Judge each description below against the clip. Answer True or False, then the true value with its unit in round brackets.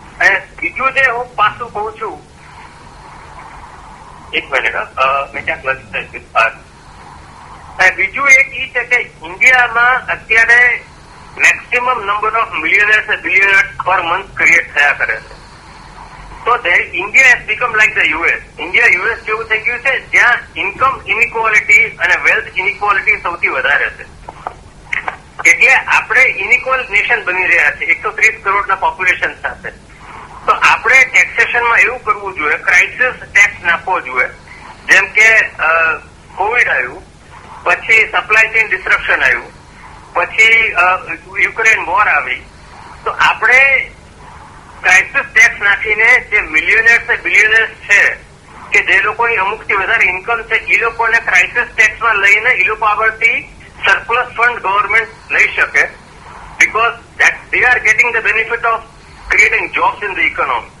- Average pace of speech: True (120 wpm)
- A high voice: True (225 Hz)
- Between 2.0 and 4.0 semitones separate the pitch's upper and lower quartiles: True (2.7 semitones)